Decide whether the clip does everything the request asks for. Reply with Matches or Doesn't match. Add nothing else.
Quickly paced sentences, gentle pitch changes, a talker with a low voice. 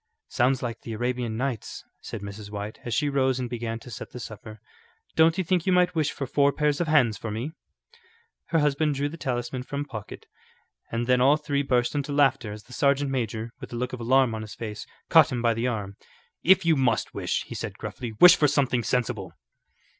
Doesn't match